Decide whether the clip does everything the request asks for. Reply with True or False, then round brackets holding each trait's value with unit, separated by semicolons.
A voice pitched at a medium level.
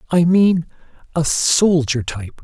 True (155 Hz)